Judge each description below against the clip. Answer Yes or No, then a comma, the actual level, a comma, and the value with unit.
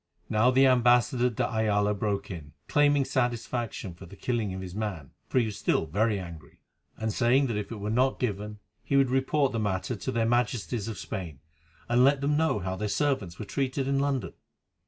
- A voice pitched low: Yes, low, 115 Hz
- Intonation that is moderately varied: Yes, average, 4.2 semitones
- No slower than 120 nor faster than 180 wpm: No, average, 200 wpm